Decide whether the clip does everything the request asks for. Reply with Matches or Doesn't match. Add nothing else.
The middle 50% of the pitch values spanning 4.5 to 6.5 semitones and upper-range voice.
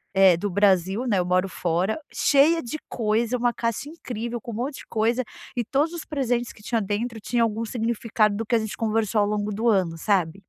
Doesn't match